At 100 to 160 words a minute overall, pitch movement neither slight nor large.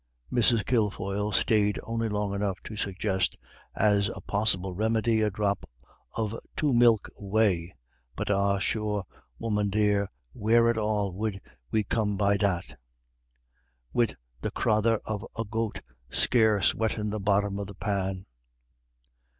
No: slow, 135 wpm; narrow, 1.8 semitones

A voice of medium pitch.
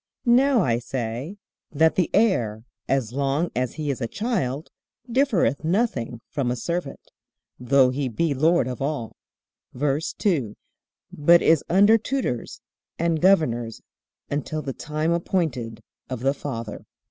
Yes: medium, 145 Hz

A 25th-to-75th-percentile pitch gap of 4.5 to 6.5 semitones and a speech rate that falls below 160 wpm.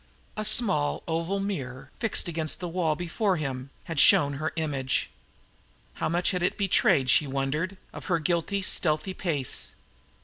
Yes: average, 4.8 semitones; average, 150 wpm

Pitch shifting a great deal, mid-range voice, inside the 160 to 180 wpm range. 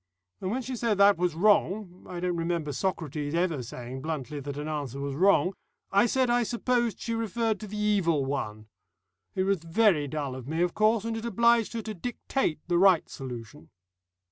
No: wide, 6.7 semitones; medium, 180 Hz; average, 195 wpm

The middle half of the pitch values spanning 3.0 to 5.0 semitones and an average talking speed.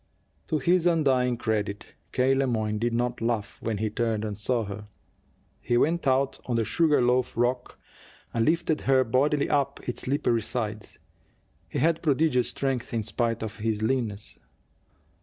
Yes: average, 3.6 semitones; average, 160 wpm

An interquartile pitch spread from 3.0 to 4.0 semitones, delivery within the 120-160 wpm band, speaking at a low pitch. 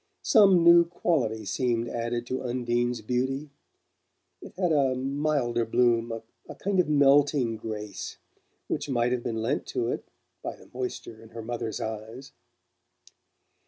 Yes: average, 3.6 semitones; average, 140 wpm; low, 125 Hz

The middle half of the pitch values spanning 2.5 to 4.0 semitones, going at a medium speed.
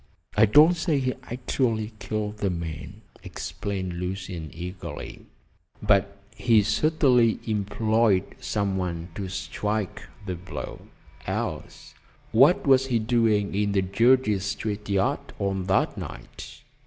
No: average, 3.3 semitones; slow, 120 wpm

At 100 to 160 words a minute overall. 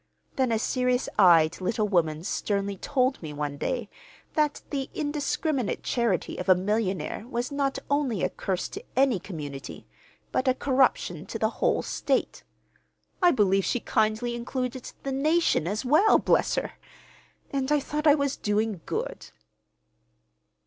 Yes: average, 150 wpm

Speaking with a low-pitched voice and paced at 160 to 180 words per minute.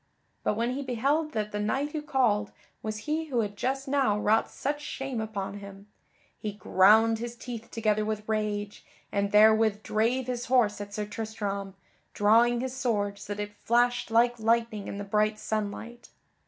No: high, 220 Hz; average, 175 wpm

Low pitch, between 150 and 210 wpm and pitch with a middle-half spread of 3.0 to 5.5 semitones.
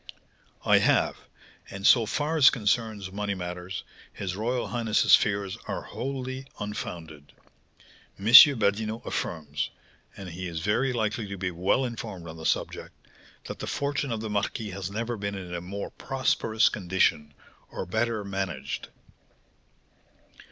No: low, 100 Hz; average, 140 wpm; average, 4.1 semitones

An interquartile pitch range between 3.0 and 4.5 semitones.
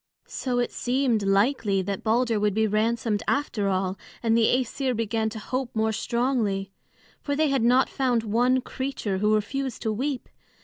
Yes: average, 3.4 semitones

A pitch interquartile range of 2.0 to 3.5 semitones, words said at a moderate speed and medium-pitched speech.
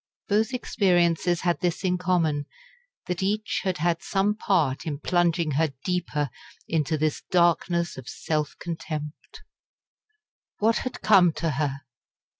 No: average, 3.1 semitones; slow, 130 wpm; medium, 170 Hz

